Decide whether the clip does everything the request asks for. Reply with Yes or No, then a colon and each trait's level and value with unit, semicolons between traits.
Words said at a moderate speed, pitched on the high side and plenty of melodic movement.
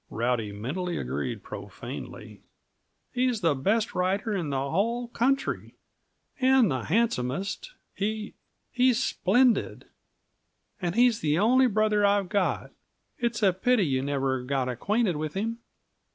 No: slow, 125 wpm; high, 200 Hz; wide, 8.6 semitones